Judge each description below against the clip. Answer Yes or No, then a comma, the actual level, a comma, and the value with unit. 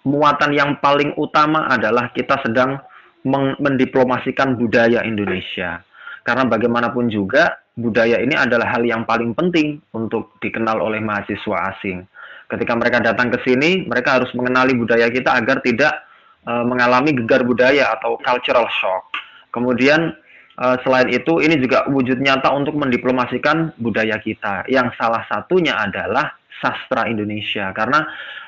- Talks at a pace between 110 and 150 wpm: Yes, average, 135 wpm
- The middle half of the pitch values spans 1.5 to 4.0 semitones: Yes, average, 2.9 semitones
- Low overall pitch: Yes, low, 125 Hz